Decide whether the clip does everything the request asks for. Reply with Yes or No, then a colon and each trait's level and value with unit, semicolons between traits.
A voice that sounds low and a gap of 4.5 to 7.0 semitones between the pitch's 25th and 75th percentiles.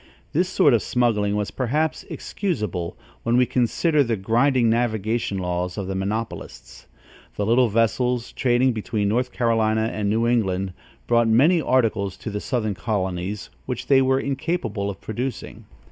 No: low, 115 Hz; average, 3.6 semitones